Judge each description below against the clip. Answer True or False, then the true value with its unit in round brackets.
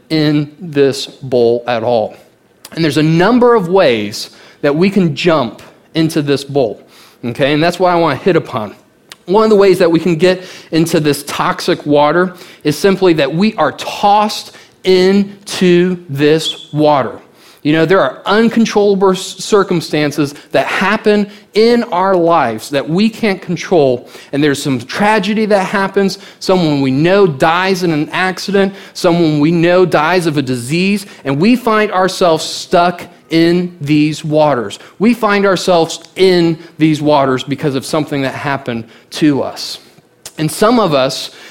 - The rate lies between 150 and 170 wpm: True (155 wpm)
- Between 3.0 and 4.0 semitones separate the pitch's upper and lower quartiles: False (4.4 semitones)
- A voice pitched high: False (170 Hz)